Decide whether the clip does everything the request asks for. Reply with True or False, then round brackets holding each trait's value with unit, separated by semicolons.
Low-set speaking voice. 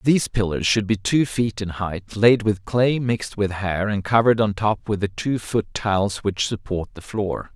True (105 Hz)